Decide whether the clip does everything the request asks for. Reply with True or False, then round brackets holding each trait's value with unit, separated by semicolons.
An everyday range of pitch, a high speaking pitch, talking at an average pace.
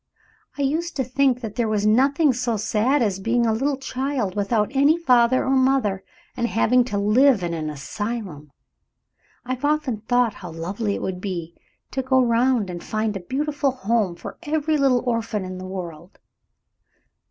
True (4.9 semitones; 235 Hz; 175 wpm)